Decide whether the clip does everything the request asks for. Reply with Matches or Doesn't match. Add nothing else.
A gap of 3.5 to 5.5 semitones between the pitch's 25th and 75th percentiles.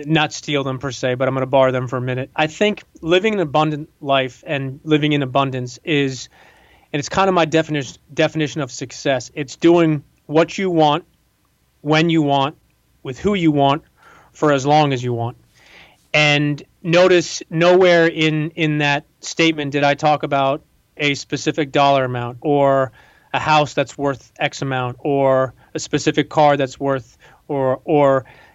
Doesn't match